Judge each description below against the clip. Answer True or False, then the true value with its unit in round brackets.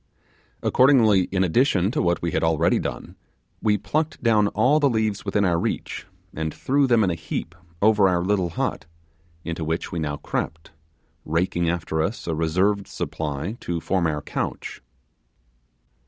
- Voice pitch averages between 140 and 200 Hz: False (90 Hz)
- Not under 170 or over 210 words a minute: False (160 wpm)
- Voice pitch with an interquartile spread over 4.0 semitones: True (4.6 semitones)